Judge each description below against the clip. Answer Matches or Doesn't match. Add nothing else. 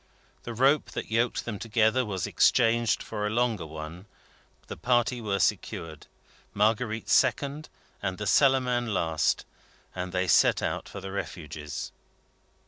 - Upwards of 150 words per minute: Doesn't match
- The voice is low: Matches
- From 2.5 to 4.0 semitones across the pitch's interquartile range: Doesn't match